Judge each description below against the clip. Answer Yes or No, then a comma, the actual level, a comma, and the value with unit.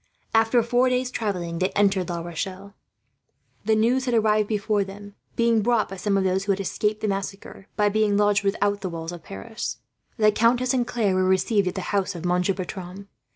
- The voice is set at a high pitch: Yes, high, 205 Hz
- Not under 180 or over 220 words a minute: Yes, average, 200 wpm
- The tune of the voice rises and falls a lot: No, average, 2.7 semitones